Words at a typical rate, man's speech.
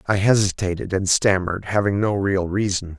Yes: average, 160 wpm; male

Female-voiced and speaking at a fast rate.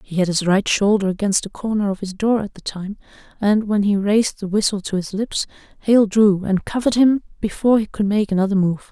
Yes: female; fast, 230 wpm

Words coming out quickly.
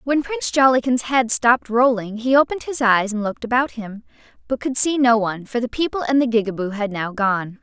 Yes: fast, 220 wpm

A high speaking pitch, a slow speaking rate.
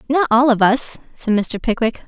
No: high, 240 Hz; average, 200 wpm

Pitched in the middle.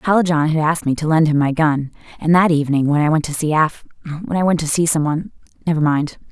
Yes: medium, 155 Hz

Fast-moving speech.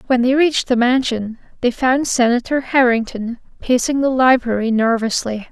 No: average, 140 wpm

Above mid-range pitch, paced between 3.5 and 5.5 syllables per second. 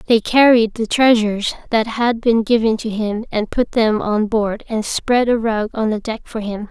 Yes: high, 225 Hz; 4.5 syllables/s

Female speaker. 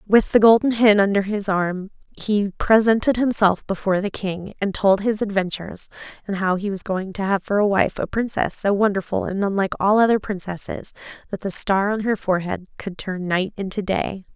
Yes: female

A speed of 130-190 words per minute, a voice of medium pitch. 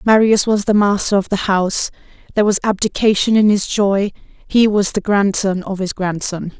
No: average, 180 wpm; high, 200 Hz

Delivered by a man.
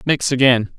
Yes: male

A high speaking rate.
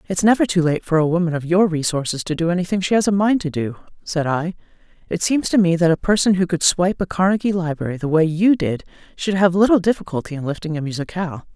Yes: fast, 240 wpm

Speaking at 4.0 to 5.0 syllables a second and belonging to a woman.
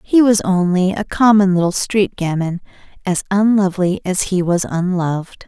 Yes: 4.8 syllables/s; female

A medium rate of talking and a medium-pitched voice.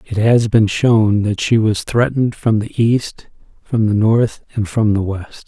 No: average, 195 wpm; low, 110 Hz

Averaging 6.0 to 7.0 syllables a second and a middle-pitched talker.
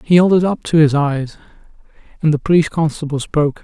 Yes: 6.3 syllables/s; medium, 155 Hz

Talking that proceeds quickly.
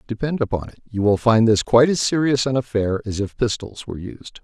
Yes: fast, 230 wpm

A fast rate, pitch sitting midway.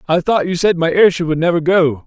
Yes: fast, 260 wpm; medium, 170 Hz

